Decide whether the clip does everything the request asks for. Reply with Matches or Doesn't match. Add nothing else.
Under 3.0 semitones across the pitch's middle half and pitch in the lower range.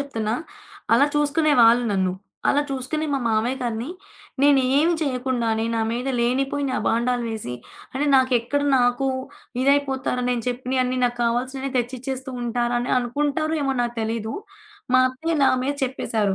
Doesn't match